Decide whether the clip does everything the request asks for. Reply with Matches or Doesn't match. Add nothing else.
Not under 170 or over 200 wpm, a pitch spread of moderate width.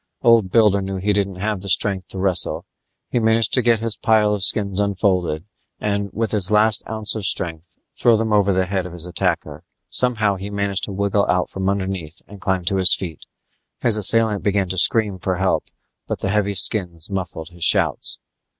Doesn't match